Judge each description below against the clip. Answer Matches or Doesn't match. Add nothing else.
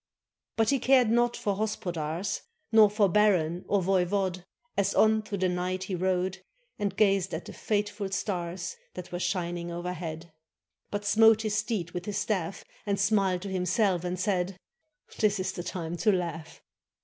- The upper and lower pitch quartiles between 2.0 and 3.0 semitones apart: Matches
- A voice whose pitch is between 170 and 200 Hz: Matches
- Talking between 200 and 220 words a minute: Doesn't match